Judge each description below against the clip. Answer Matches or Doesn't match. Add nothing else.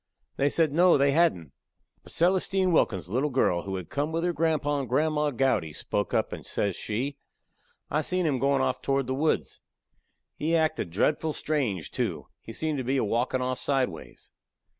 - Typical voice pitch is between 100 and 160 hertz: Matches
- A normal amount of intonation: Matches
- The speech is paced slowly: Doesn't match